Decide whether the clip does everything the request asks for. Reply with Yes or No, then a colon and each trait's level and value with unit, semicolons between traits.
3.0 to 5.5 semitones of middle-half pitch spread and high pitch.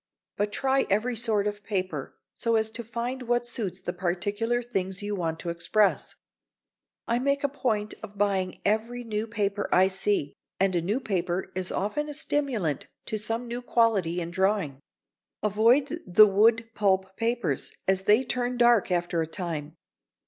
Yes: average, 4.0 semitones; high, 210 Hz